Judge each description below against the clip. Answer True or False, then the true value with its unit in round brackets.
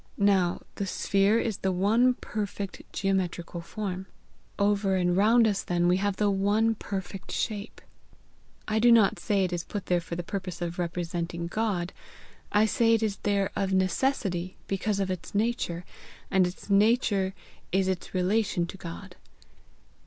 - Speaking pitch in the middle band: False (195 Hz)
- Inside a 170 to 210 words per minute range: False (160 wpm)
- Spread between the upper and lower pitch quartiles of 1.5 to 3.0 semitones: True (2.7 semitones)